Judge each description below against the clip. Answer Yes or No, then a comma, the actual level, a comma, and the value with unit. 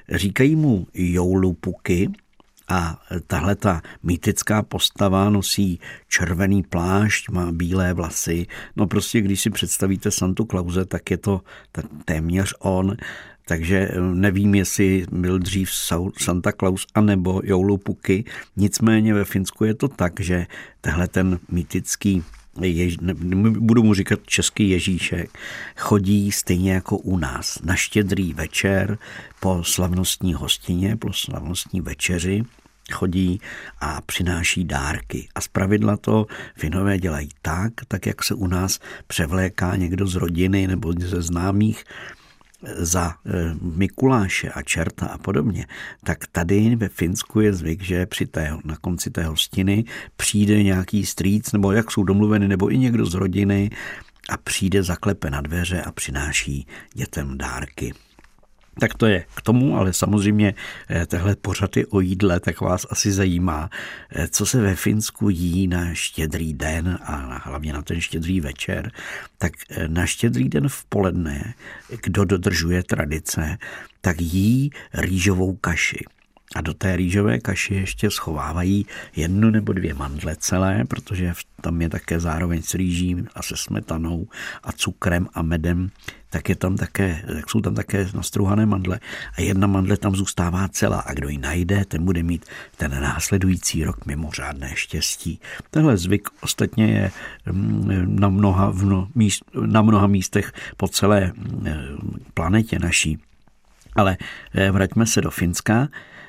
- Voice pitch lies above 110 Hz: No, very low, 95 Hz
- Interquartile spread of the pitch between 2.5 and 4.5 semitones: Yes, average, 2.8 semitones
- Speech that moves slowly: No, average, 140 wpm